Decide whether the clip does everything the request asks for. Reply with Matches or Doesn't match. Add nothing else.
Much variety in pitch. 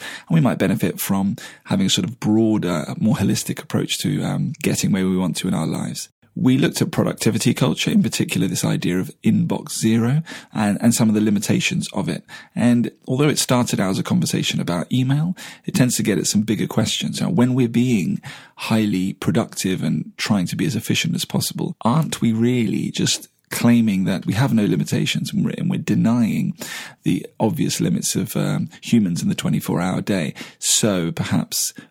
Matches